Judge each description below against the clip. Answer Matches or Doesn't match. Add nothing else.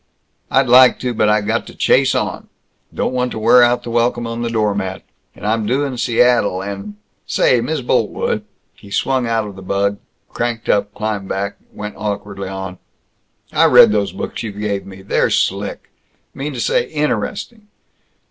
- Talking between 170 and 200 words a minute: Matches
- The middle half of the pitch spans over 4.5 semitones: Doesn't match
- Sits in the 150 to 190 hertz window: Doesn't match